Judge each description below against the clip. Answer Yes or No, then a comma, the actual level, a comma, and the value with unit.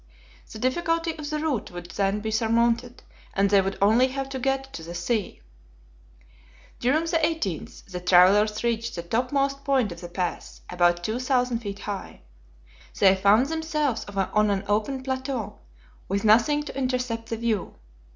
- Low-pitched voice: No, high, 230 Hz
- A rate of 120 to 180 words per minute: Yes, average, 160 wpm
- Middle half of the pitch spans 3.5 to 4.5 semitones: No, average, 5.2 semitones